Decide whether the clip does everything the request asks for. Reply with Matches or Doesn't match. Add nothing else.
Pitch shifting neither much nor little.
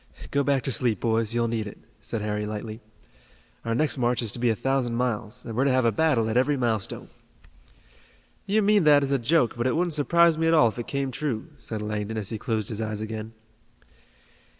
Matches